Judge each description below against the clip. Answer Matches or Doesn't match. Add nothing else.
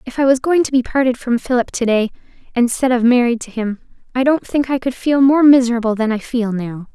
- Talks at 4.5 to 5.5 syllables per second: Doesn't match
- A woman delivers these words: Matches